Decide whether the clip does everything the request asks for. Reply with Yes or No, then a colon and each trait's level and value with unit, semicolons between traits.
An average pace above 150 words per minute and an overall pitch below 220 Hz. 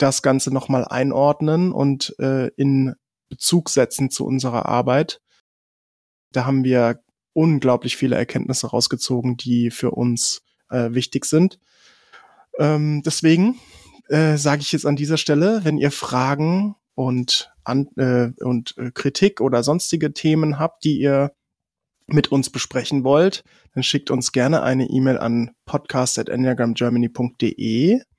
No: average, 130 wpm; low, 135 Hz